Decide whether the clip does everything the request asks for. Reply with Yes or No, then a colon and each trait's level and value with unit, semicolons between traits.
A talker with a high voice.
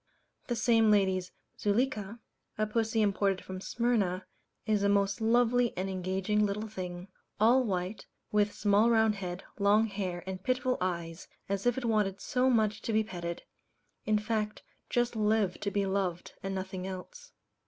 Yes: high, 205 Hz